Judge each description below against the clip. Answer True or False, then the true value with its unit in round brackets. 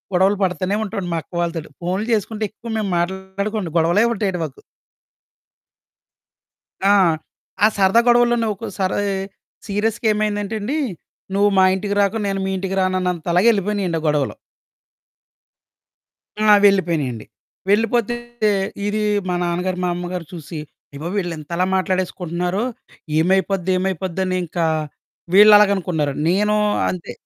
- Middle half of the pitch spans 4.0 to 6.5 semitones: False (2.8 semitones)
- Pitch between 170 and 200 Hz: True (190 Hz)